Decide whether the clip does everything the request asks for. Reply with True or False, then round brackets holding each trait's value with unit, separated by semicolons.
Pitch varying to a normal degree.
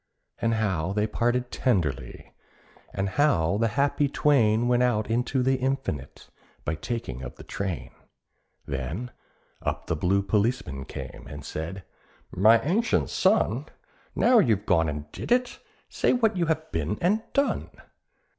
False (8.3 semitones)